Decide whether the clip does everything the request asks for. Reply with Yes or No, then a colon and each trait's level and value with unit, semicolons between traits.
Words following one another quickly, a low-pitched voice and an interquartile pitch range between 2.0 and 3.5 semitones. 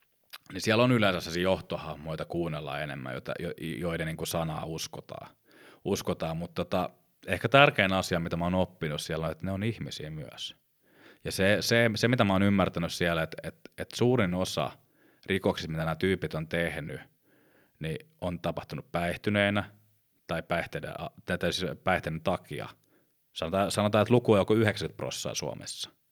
No: fast, 160 wpm; very low, 95 Hz; average, 4.4 semitones